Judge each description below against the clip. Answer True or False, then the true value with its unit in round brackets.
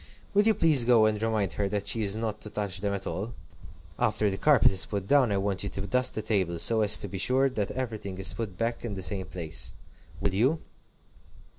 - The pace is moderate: False (235 wpm)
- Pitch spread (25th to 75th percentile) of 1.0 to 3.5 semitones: True (3.1 semitones)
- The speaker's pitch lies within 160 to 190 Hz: False (105 Hz)